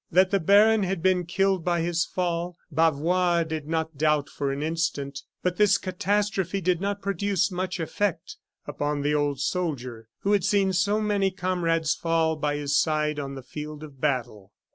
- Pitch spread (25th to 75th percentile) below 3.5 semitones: No, average, 4.0 semitones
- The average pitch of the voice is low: No, medium, 165 Hz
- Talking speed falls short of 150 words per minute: No, average, 175 wpm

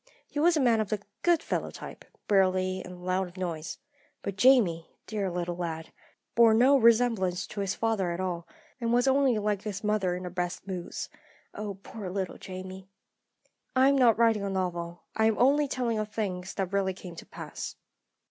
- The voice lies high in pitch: Yes, high, 195 Hz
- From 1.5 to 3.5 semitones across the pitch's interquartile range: No, average, 3.9 semitones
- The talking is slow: No, average, 190 wpm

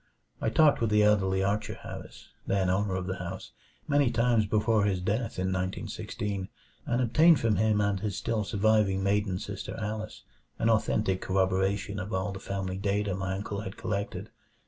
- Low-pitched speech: Yes, low, 100 Hz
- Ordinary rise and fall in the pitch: No, narrow, 2.3 semitones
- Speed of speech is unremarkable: Yes, average, 170 wpm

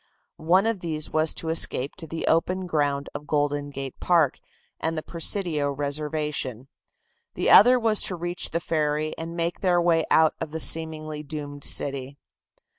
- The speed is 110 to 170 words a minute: Yes, average, 165 wpm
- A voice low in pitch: No, medium, 155 Hz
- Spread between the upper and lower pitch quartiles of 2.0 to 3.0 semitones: Yes, narrow, 2.6 semitones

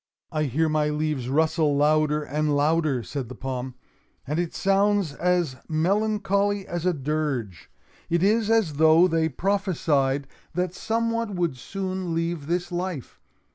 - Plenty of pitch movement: No, average, 4.1 semitones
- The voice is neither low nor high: Yes, medium, 160 Hz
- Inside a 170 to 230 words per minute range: No, average, 145 wpm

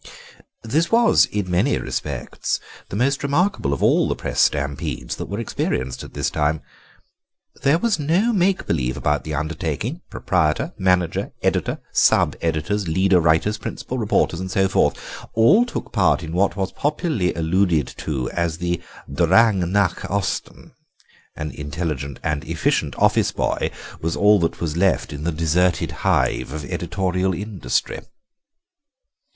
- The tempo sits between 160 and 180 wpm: No, average, 145 wpm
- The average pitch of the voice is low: Yes, very low, 90 Hz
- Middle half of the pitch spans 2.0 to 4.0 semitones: No, average, 5.1 semitones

